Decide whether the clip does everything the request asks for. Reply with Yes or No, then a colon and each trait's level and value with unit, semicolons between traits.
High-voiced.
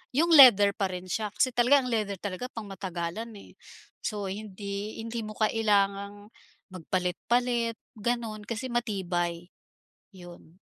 Yes: high, 210 Hz